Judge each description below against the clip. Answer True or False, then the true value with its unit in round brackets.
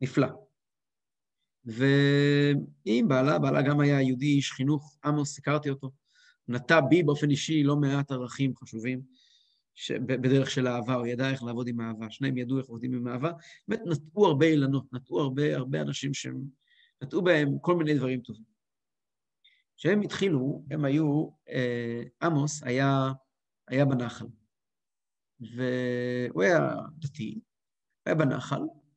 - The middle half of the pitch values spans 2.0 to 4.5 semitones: True (2.8 semitones)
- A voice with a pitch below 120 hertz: False (135 Hz)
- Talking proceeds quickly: False (135 wpm)